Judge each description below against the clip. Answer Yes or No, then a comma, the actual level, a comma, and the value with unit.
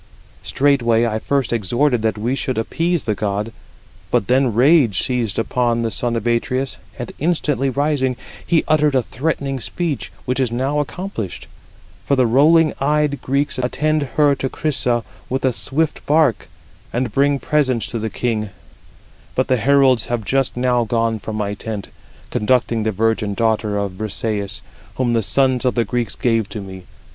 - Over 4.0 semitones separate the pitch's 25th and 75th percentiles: No, average, 3.7 semitones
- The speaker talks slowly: No, average, 165 wpm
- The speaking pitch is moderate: No, low, 125 Hz